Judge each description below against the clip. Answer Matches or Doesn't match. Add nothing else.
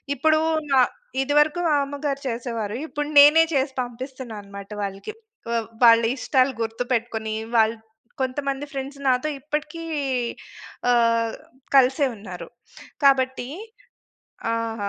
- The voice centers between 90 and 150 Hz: Doesn't match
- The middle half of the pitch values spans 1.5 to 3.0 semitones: Doesn't match